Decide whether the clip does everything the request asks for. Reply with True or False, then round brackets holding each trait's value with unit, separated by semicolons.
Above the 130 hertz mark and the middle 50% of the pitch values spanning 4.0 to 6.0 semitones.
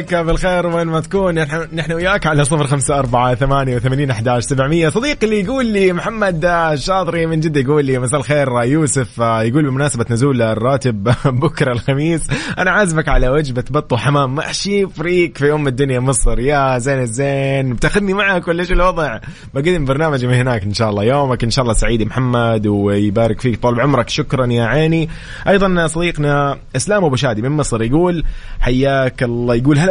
True (140 Hz; 4.8 semitones)